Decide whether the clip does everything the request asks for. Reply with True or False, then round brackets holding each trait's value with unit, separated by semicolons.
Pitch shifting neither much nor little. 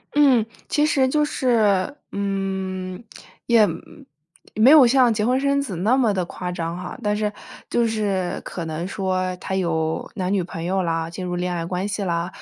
True (4.5 semitones)